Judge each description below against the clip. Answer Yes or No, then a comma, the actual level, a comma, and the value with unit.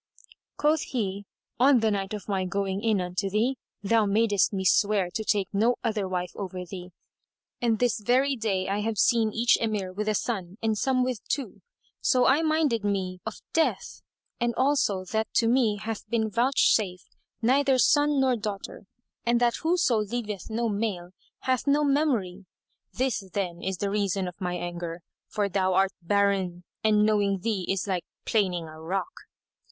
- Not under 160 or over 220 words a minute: Yes, average, 170 wpm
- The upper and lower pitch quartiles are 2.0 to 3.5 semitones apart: No, average, 3.9 semitones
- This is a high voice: Yes, high, 210 Hz